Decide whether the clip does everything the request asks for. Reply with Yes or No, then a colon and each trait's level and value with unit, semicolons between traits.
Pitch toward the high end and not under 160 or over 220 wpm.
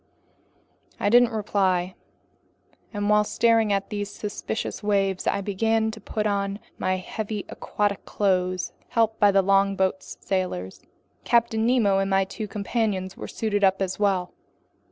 No: high, 200 Hz; slow, 135 wpm